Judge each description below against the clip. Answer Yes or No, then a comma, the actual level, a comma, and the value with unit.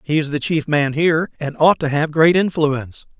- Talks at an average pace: No, fast, 225 wpm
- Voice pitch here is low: No, medium, 150 Hz